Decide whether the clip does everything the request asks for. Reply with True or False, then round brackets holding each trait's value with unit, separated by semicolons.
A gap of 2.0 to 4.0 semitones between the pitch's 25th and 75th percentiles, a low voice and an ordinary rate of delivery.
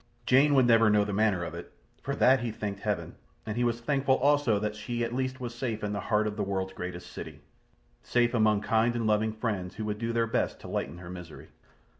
False (2.7 semitones; 110 Hz; 235 wpm)